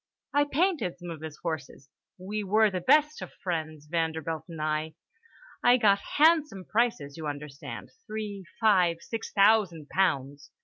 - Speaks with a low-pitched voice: No, medium, 180 Hz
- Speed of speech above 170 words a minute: No, average, 145 wpm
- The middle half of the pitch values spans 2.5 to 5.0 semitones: No, wide, 5.6 semitones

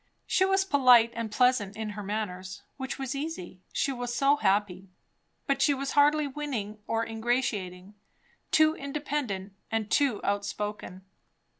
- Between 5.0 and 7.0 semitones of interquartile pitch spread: Yes, average, 5.3 semitones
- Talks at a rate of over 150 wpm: No, average, 140 wpm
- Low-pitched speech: No, high, 230 Hz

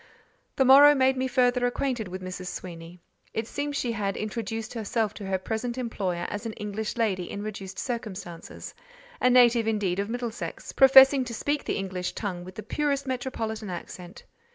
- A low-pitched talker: No, high, 220 Hz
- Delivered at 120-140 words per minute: No, average, 175 wpm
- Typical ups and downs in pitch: Yes, average, 4.5 semitones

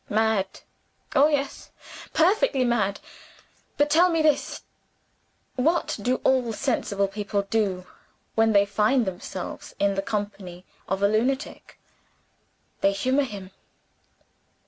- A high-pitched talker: Yes, high, 220 Hz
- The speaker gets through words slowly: Yes, slow, 115 wpm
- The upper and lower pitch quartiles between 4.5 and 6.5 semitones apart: Yes, wide, 5.4 semitones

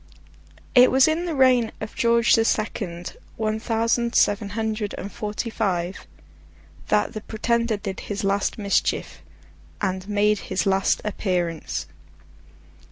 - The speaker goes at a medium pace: No, slow, 130 wpm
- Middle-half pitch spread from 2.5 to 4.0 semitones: Yes, average, 2.8 semitones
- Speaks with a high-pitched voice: Yes, high, 215 Hz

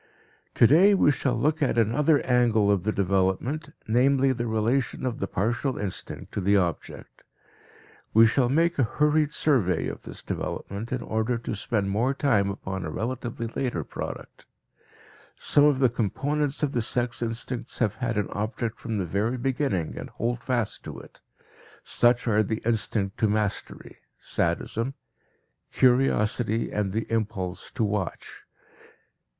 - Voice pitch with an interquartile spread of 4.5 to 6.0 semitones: No, average, 3.9 semitones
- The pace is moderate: Yes, average, 150 wpm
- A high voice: No, low, 115 Hz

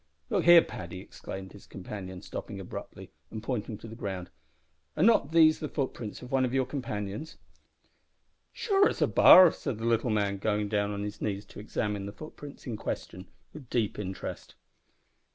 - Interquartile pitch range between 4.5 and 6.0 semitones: Yes, average, 5.1 semitones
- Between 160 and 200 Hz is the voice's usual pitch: No, low, 110 Hz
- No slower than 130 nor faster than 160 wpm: No, average, 175 wpm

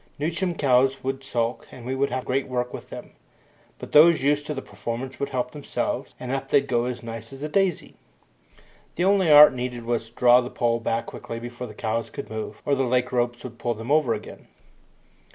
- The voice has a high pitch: No, low, 125 Hz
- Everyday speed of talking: No, fast, 220 wpm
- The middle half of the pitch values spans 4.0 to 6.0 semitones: No, average, 2.8 semitones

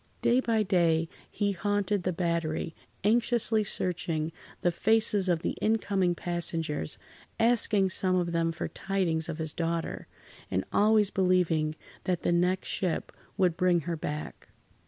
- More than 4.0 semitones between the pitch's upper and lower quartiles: No, average, 3.4 semitones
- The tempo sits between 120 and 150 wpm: Yes, average, 140 wpm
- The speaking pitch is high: No, medium, 180 Hz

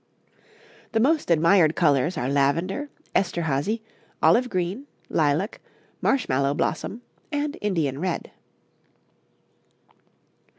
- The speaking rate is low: Yes, slow, 85 wpm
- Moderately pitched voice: Yes, medium, 175 Hz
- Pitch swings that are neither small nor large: No, wide, 7.4 semitones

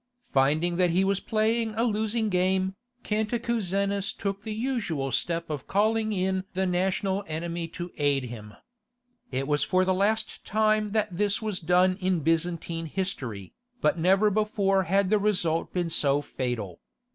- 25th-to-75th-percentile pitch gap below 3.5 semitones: No, average, 4.2 semitones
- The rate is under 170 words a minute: Yes, average, 155 wpm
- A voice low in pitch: No, medium, 185 Hz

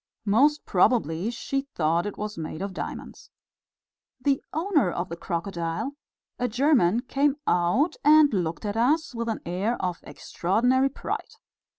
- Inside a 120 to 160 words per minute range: Yes, average, 145 wpm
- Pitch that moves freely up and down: Yes, wide, 7.5 semitones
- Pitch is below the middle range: No, high, 225 Hz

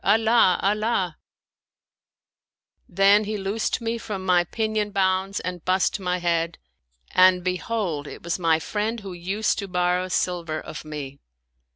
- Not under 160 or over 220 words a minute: No, average, 145 wpm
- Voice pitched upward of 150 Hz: Yes, medium, 185 Hz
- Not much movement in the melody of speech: No, average, 3.1 semitones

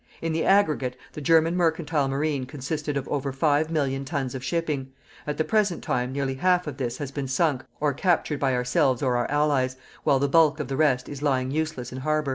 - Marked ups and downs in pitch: No, average, 3.0 semitones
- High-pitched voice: No, medium, 145 Hz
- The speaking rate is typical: No, fast, 215 wpm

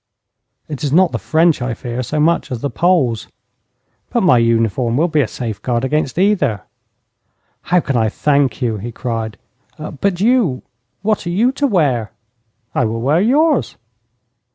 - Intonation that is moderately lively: No, wide, 7.0 semitones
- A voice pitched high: No, medium, 140 Hz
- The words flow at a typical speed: Yes, average, 160 wpm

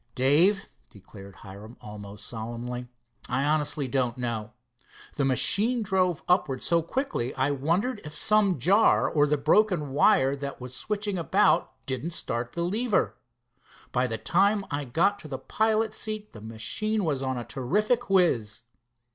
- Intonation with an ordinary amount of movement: No, wide, 8.3 semitones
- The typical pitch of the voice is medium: Yes, medium, 145 Hz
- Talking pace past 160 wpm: No, average, 150 wpm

